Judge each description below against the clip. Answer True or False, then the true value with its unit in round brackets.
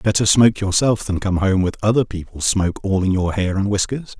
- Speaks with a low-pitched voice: True (100 Hz)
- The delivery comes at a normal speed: False (230 wpm)